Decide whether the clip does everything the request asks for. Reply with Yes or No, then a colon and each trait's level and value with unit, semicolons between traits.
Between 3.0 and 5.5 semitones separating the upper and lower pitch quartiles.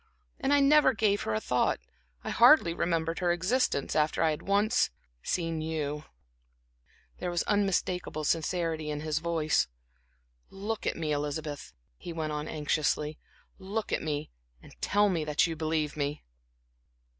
Yes: average, 4.1 semitones